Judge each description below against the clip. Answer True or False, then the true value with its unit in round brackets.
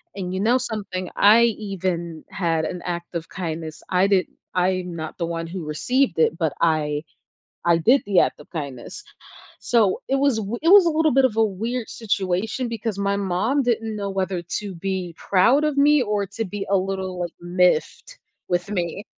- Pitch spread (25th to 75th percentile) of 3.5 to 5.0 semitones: True (4.5 semitones)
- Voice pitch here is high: True (195 Hz)